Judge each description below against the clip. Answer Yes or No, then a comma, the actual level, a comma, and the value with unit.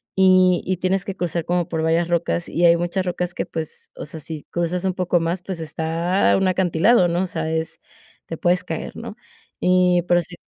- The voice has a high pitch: No, medium, 175 Hz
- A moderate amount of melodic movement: No, narrow, 1.7 semitones